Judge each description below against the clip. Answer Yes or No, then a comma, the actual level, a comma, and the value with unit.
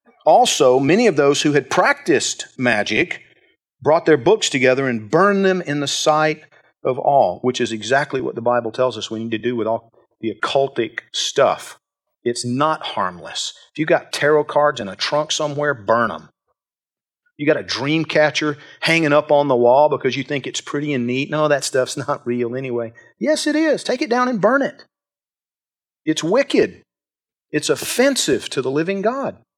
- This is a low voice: No, medium, 145 Hz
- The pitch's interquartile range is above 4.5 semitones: No, average, 3.7 semitones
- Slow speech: No, average, 185 wpm